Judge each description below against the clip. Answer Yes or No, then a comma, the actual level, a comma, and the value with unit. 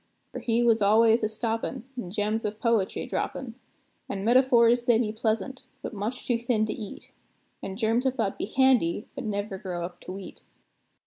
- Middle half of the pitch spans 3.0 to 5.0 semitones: No, narrow, 2.6 semitones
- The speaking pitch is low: No, high, 225 Hz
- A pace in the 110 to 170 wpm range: No, average, 185 wpm